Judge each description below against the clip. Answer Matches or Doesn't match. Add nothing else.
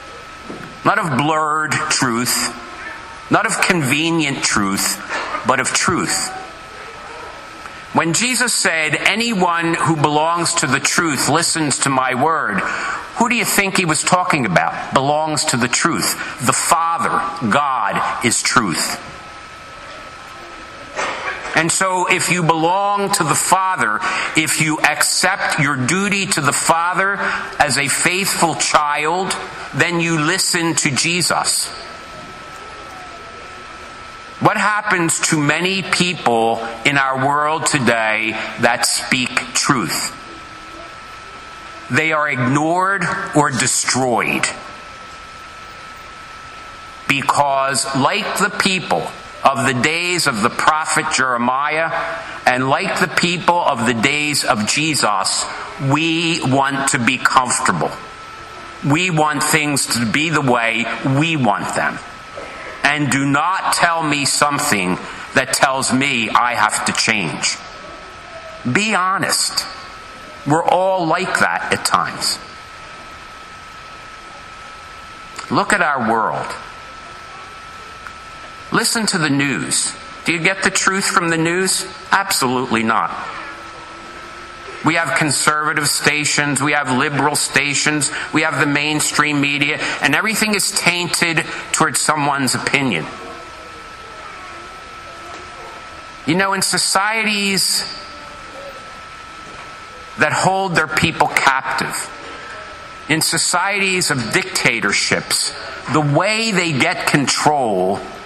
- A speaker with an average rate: Doesn't match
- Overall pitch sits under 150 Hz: Doesn't match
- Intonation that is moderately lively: Matches